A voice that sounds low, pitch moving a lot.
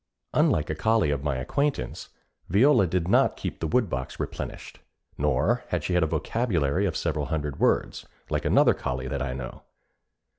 Yes: very low, 80 Hz; wide, 6.2 semitones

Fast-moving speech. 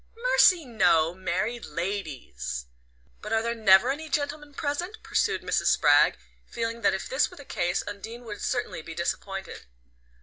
No: average, 155 wpm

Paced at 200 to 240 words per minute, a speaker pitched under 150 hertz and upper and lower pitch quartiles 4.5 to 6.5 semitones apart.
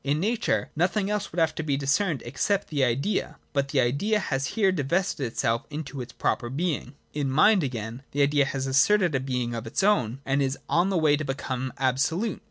Yes: fast, 205 wpm; medium, 140 Hz; average, 5.3 semitones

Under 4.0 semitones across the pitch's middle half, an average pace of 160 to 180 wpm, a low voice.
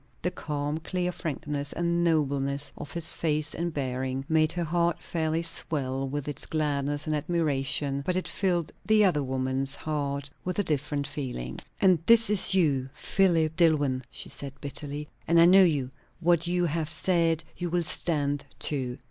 No: average, 3.3 semitones; average, 165 wpm; medium, 155 Hz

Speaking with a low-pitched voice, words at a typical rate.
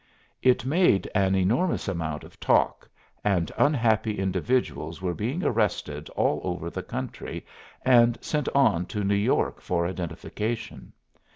No: low, 105 Hz; slow, 130 wpm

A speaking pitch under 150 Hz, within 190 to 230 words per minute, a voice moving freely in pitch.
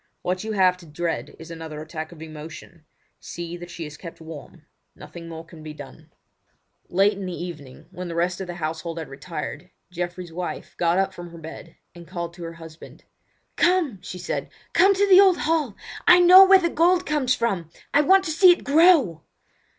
No: medium, 175 Hz; average, 200 wpm; wide, 8.9 semitones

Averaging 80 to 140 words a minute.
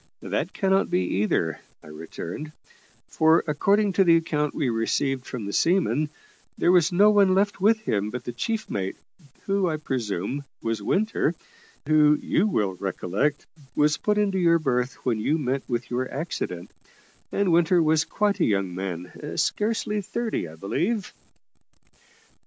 No: average, 155 wpm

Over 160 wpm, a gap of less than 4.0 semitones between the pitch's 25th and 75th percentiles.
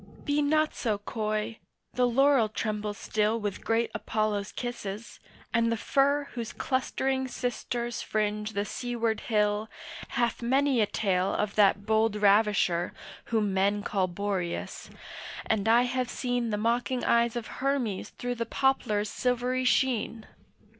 No: average, 140 wpm; average, 2.9 semitones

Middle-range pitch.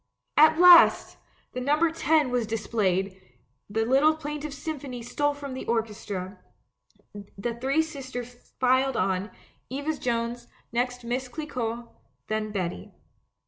No: very high, 250 Hz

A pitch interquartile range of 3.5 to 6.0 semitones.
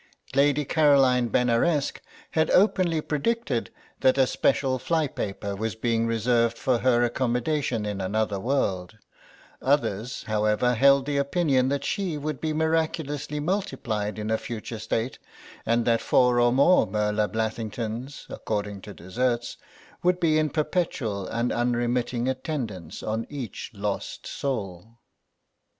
Yes: average, 4.5 semitones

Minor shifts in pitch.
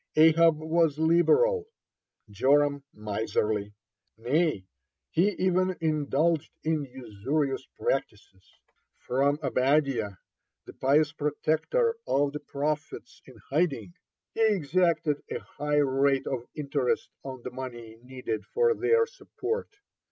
No: average, 4.2 semitones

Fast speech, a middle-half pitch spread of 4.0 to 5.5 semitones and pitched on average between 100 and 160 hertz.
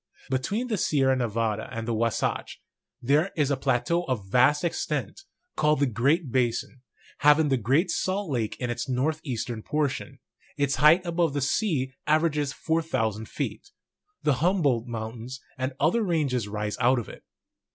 No: average, 160 wpm; average, 4.6 semitones; low, 135 Hz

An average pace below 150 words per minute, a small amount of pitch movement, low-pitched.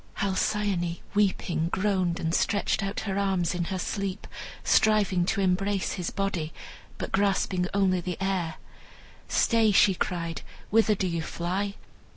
No: average, 140 wpm; narrow, 2.3 semitones; high, 190 Hz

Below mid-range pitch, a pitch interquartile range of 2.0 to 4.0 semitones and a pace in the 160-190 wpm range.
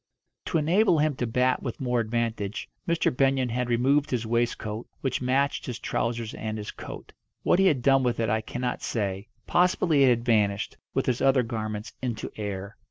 Yes: low, 120 Hz; average, 3.4 semitones; average, 185 wpm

